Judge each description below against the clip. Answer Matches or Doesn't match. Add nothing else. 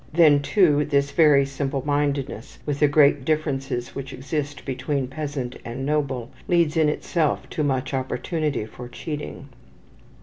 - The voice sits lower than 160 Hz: Matches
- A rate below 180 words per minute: Matches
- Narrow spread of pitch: Matches